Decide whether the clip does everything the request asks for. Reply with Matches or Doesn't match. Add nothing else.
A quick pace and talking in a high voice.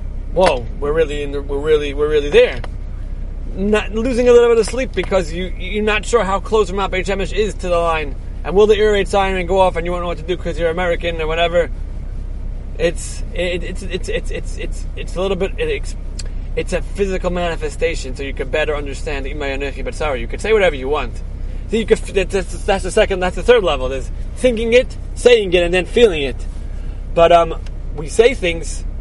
Matches